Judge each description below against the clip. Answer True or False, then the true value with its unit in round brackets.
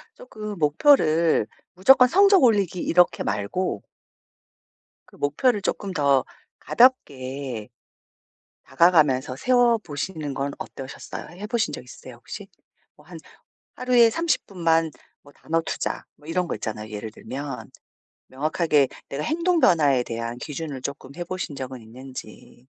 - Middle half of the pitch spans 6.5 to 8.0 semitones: True (7.6 semitones)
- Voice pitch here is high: False (155 Hz)